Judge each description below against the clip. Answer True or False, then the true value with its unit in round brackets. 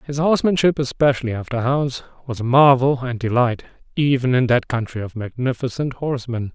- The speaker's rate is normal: True (155 wpm)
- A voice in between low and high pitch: False (130 Hz)